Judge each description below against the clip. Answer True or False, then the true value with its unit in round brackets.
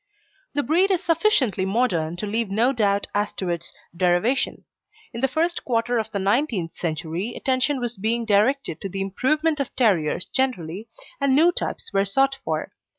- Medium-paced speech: True (170 wpm)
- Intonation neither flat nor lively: False (5.8 semitones)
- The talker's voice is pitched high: True (230 Hz)